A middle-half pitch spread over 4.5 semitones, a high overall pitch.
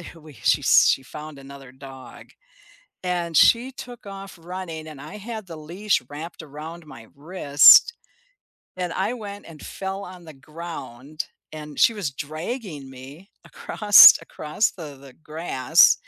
No: average, 4.9 semitones; medium, 160 Hz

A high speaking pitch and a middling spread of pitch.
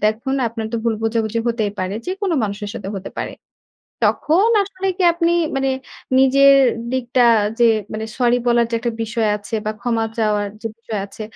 Yes: high, 235 Hz; average, 3.5 semitones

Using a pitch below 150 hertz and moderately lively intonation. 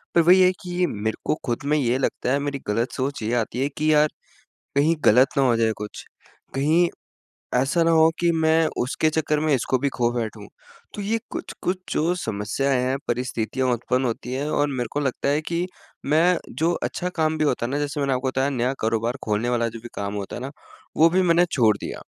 Yes: medium, 140 Hz; average, 4.7 semitones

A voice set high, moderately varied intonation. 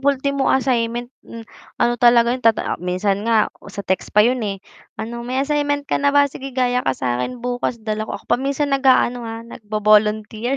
Yes: high, 240 Hz; average, 3.6 semitones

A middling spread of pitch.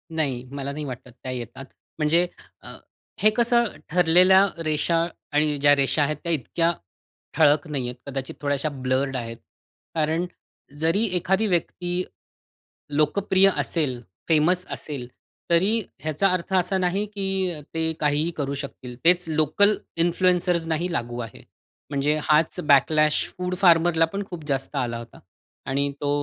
Yes: average, 4.1 semitones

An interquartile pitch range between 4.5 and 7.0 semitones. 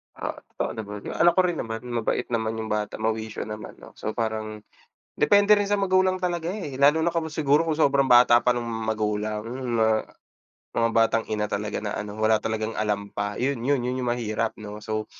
Yes: average, 5.1 semitones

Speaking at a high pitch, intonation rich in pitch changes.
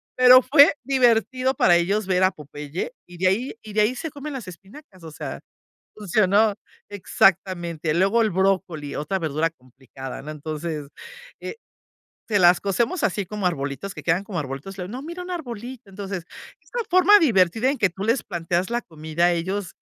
Yes: high, 195 Hz; wide, 5.7 semitones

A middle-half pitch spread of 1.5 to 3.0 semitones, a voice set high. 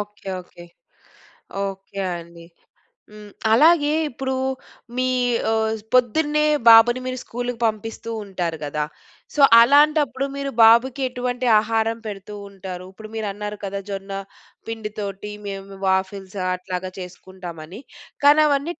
No: average, 4.6 semitones; high, 215 Hz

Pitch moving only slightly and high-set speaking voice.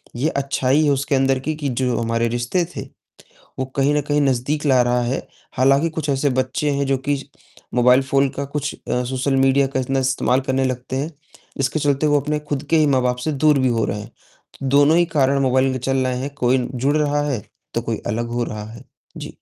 No: narrow, 2.2 semitones; low, 135 Hz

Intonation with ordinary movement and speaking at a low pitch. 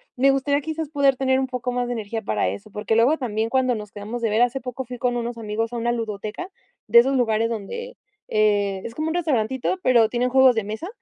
No: average, 3.3 semitones; high, 240 Hz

